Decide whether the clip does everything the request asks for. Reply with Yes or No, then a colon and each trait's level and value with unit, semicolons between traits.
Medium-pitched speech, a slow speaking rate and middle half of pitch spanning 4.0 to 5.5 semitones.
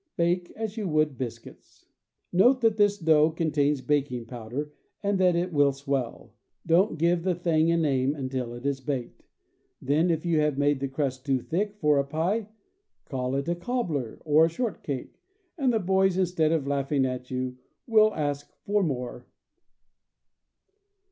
No: medium, 155 Hz; average, 165 wpm; average, 4.7 semitones